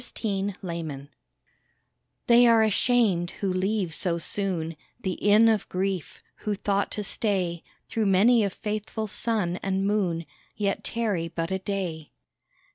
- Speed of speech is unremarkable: No, slow, 130 wpm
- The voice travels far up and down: No, average, 3.4 semitones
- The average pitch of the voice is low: No, high, 195 Hz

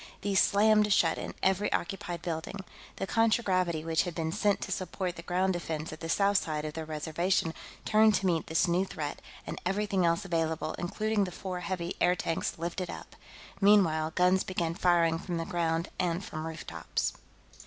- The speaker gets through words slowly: No, average, 175 wpm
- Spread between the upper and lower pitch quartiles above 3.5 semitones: No, average, 2.9 semitones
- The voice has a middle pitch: Yes, medium, 175 Hz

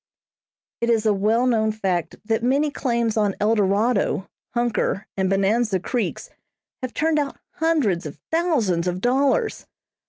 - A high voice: Yes, high, 225 Hz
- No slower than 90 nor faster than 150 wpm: Yes, slow, 135 wpm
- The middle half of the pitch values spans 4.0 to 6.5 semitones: Yes, average, 4.6 semitones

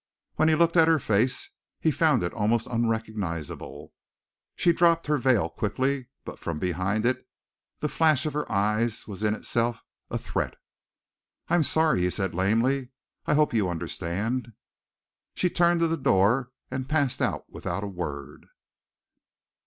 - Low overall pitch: Yes, low, 120 Hz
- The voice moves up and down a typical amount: No, wide, 7.1 semitones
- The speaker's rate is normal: Yes, average, 155 wpm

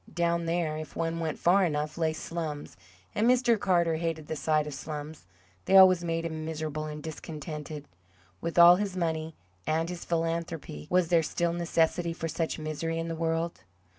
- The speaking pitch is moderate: Yes, medium, 165 Hz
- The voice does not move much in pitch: Yes, narrow, 1.6 semitones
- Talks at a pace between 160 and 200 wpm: Yes, average, 175 wpm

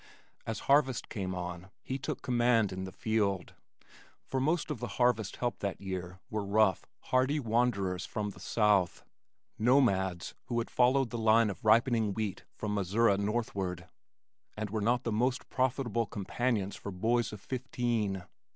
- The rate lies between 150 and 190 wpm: Yes, average, 155 wpm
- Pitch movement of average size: Yes, average, 3.8 semitones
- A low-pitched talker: Yes, low, 110 Hz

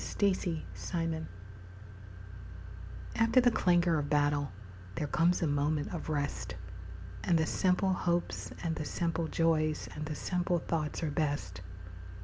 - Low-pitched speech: No, medium, 160 Hz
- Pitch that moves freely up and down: No, average, 2.7 semitones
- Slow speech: Yes, slow, 125 wpm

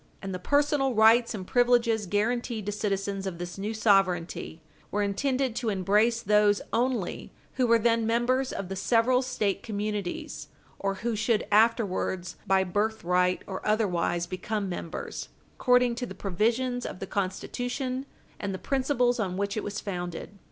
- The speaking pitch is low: No, high, 210 Hz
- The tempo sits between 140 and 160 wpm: Yes, average, 155 wpm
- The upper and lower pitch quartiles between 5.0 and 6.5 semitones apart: No, average, 3.8 semitones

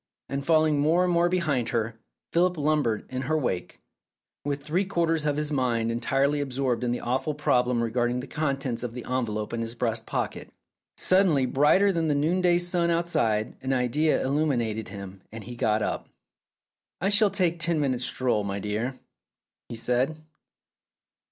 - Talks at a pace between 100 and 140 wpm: No, average, 165 wpm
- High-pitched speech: No, low, 135 Hz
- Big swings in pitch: No, average, 5.0 semitones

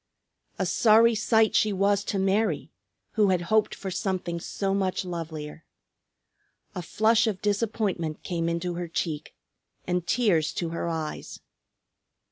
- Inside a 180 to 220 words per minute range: No, slow, 135 wpm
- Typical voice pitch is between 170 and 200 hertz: Yes, high, 190 Hz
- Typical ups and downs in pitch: Yes, average, 3.8 semitones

